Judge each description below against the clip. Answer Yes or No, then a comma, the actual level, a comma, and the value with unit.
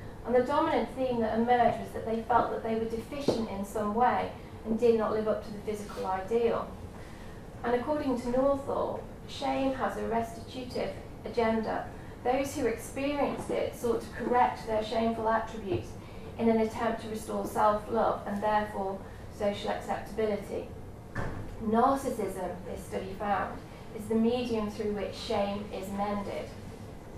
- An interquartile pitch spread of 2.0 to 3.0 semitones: Yes, average, 2.7 semitones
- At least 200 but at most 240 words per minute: No, average, 150 wpm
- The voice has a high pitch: Yes, high, 225 Hz